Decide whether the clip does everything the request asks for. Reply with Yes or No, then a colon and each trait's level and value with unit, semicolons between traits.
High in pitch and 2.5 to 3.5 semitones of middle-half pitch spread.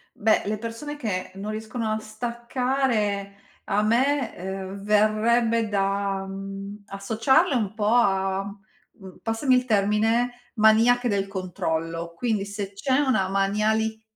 Yes: high, 215 Hz; average, 2.9 semitones